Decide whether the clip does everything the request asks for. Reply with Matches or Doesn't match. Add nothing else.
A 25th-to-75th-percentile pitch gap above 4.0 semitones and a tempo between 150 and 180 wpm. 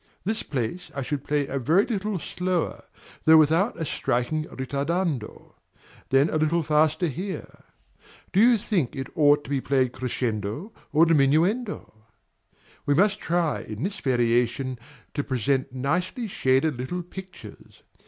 Doesn't match